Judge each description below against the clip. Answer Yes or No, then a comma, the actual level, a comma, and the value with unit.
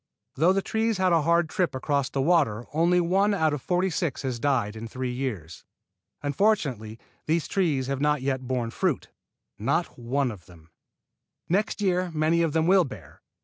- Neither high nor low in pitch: Yes, medium, 150 Hz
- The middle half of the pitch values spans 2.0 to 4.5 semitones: No, wide, 5.6 semitones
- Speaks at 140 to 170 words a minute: No, average, 180 wpm